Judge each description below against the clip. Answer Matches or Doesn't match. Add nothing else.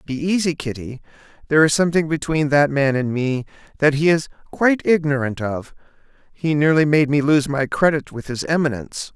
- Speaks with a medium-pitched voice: Matches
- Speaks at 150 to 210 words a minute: Matches